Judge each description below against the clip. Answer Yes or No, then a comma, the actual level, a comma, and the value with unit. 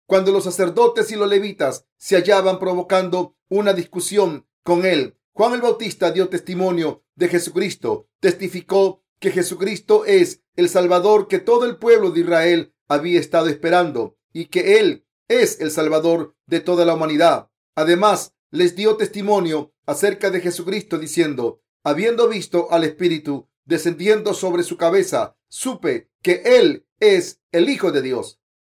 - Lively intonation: No, average, 4.1 semitones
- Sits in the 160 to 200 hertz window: Yes, medium, 185 Hz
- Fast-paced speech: No, average, 145 wpm